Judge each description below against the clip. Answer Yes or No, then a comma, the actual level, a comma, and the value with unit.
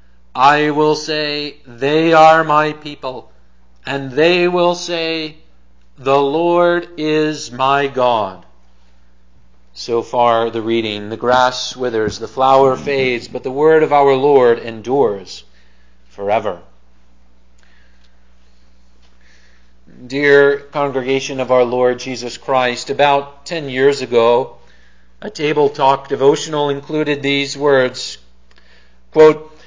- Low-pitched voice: Yes, low, 130 Hz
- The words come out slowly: Yes, slow, 105 wpm